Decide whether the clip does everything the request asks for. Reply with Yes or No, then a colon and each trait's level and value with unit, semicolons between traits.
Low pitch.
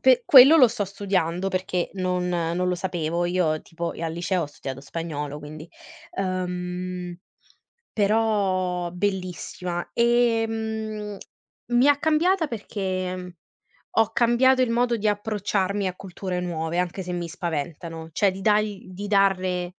No: medium, 185 Hz